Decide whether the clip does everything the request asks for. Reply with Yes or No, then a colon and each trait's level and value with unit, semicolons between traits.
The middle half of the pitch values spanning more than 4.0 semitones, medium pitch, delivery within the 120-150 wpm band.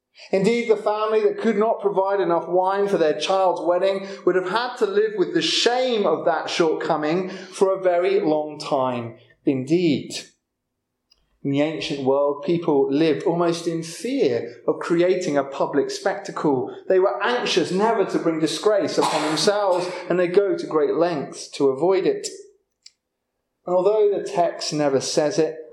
No: wide, 5.4 semitones; medium, 180 Hz; average, 160 wpm